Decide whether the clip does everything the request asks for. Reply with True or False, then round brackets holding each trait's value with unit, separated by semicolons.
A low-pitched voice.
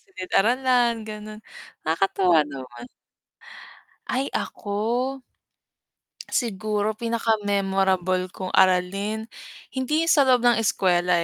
False (210 Hz)